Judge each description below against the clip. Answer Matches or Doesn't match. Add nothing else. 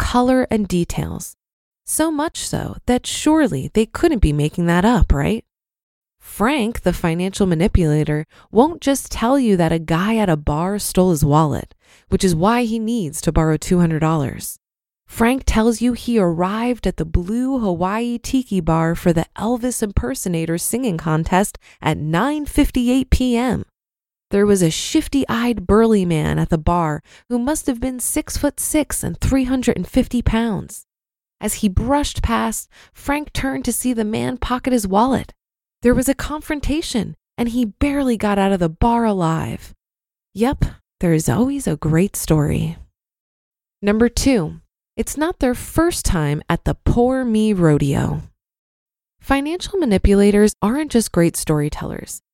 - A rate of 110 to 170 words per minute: Matches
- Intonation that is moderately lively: Doesn't match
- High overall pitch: Matches